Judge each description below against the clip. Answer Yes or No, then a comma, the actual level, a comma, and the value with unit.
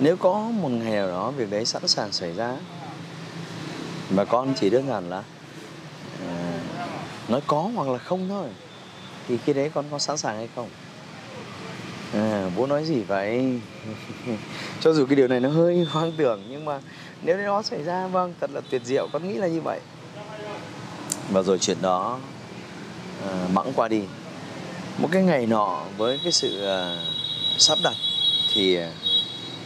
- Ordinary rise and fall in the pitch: No, wide, 6.8 semitones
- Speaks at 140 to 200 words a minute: Yes, average, 170 wpm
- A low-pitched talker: No, medium, 145 Hz